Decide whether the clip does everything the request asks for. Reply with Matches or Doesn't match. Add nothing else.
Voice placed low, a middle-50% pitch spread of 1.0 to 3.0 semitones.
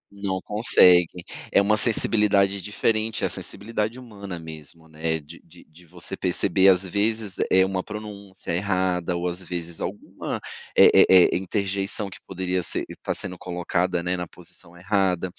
Matches